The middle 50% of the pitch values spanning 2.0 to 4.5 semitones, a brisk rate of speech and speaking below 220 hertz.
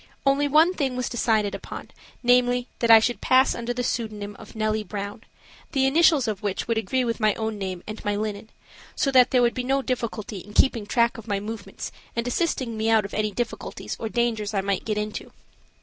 No: average, 2.9 semitones; fast, 210 wpm; high, 225 Hz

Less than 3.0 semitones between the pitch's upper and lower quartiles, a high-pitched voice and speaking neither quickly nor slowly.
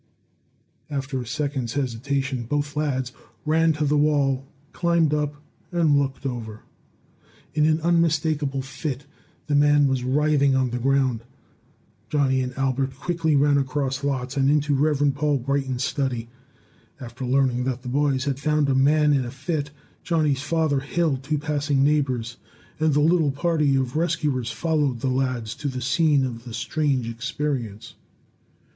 No: narrow, 2.4 semitones; medium, 140 Hz; average, 150 wpm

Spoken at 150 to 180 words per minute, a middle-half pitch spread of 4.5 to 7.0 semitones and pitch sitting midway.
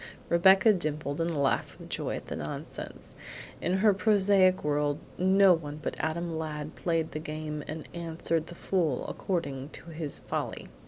No: average, 160 wpm; average, 3.4 semitones; medium, 165 Hz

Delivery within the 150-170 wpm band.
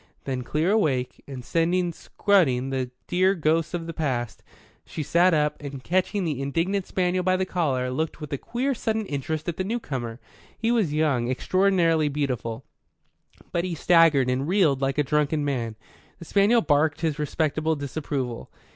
Yes: average, 165 wpm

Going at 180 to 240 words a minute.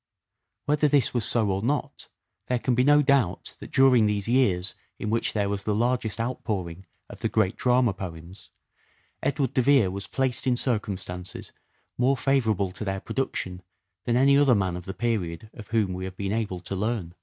Yes: average, 190 wpm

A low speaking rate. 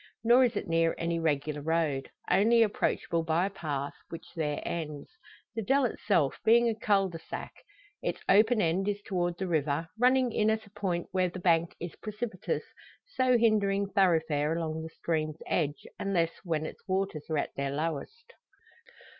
No: average, 170 wpm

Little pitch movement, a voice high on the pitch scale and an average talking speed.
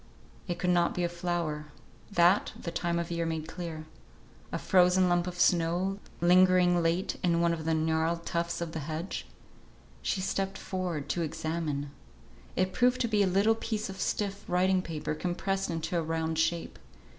No: narrow, 2.2 semitones; medium, 175 Hz; average, 175 wpm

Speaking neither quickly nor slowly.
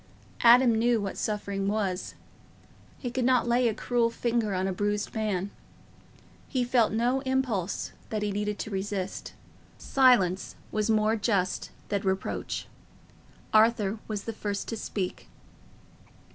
No: slow, 130 wpm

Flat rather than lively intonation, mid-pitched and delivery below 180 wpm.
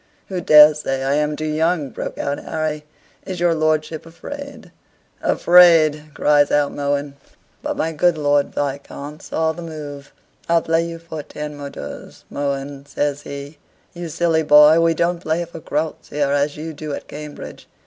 Yes: narrow, 2.3 semitones; medium, 150 Hz; average, 165 wpm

